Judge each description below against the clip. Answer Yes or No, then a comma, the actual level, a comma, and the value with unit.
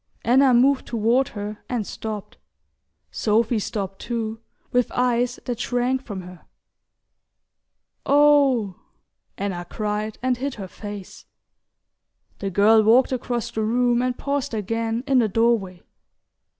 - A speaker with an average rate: No, slow, 125 wpm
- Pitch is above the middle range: Yes, high, 230 Hz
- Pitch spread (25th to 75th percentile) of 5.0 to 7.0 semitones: No, average, 3.1 semitones